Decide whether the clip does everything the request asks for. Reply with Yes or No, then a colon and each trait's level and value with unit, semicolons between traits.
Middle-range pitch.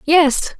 No: very high, 310 Hz